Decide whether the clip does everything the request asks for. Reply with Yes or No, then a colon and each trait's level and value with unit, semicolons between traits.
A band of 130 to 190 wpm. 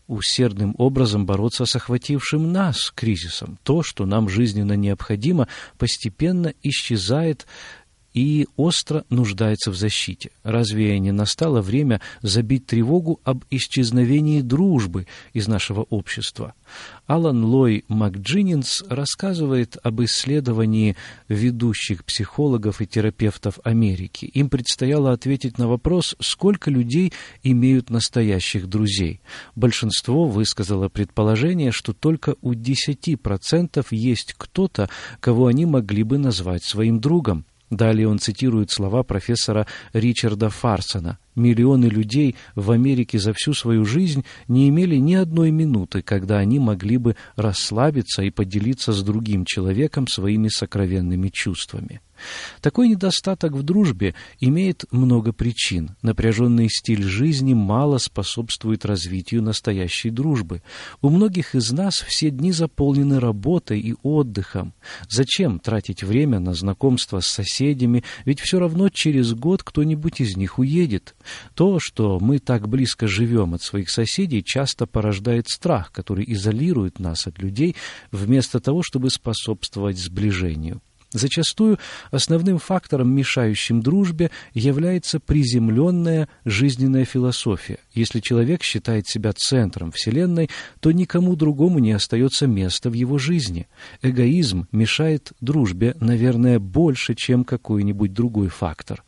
No: average, 120 wpm